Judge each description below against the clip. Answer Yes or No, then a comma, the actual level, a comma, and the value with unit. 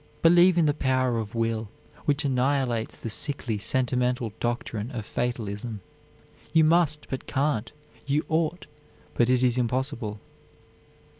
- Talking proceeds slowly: Yes, slow, 130 wpm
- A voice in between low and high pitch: No, low, 125 Hz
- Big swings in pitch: No, average, 4.1 semitones